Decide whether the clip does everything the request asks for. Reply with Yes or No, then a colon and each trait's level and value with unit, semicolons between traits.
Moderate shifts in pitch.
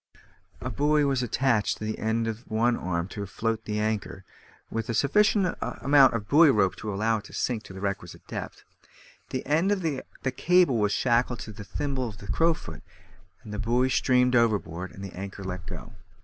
Yes: average, 4.6 semitones